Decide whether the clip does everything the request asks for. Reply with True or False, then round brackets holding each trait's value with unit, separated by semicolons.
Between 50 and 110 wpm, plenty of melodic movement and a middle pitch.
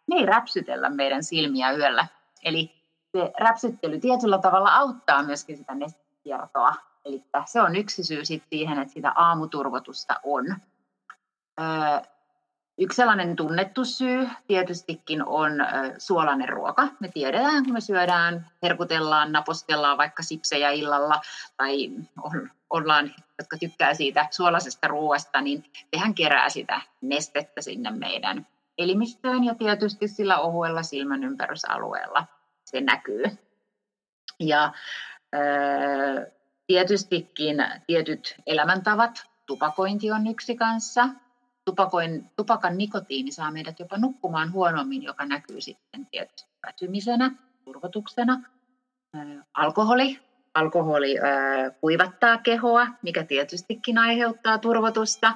True (105 wpm; 7.5 semitones; 170 Hz)